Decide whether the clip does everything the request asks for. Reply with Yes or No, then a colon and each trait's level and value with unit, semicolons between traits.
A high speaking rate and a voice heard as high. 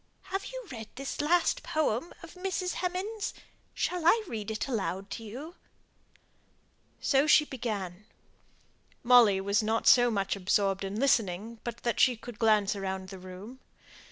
No: average, 150 wpm; high, 230 Hz